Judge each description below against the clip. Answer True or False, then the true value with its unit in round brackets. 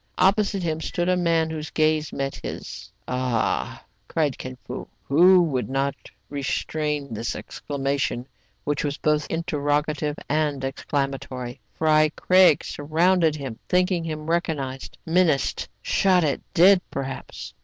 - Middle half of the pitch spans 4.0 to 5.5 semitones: False (3.3 semitones)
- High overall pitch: False (150 Hz)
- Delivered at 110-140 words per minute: True (135 wpm)